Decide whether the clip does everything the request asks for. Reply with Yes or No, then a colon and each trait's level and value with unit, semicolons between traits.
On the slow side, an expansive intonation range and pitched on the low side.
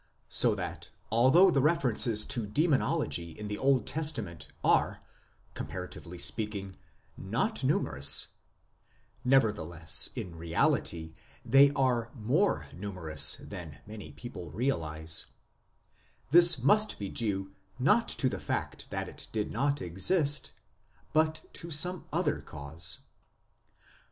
Yes: slow, 110 wpm; wide, 8.6 semitones; low, 110 Hz